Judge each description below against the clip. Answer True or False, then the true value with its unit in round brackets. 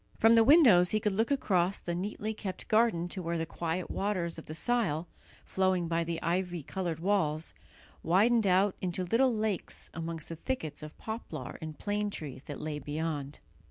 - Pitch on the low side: False (180 Hz)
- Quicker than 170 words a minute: True (180 wpm)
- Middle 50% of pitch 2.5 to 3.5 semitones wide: False (4.3 semitones)